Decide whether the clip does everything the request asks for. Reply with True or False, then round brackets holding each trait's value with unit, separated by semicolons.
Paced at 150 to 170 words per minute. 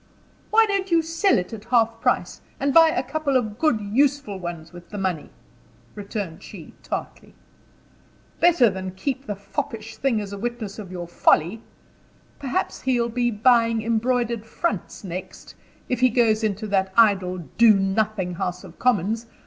True (165 wpm)